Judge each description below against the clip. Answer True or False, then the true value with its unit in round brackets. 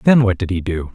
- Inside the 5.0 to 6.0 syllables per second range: True (5.5 syllables/s)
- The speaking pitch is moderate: False (100 Hz)